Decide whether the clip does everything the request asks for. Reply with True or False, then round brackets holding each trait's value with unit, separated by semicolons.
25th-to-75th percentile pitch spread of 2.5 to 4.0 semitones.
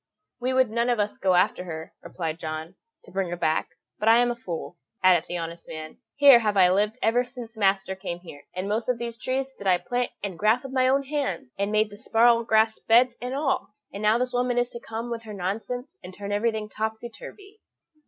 False (4.4 semitones)